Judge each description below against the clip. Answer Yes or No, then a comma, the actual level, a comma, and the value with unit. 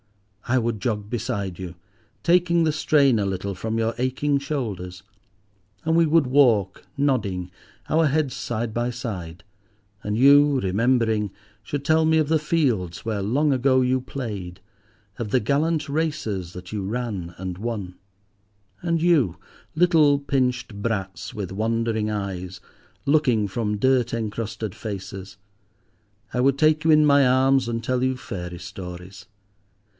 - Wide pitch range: Yes, wide, 6.0 semitones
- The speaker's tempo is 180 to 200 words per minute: No, average, 145 wpm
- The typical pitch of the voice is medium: No, low, 120 Hz